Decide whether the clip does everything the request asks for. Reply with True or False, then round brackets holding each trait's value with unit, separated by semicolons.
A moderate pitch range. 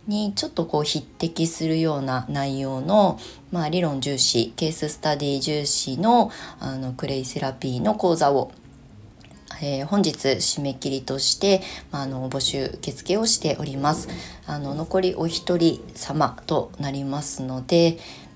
True (3.7 semitones)